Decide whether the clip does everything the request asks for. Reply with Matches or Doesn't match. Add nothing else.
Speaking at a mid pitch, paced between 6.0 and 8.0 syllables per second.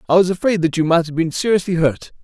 Matches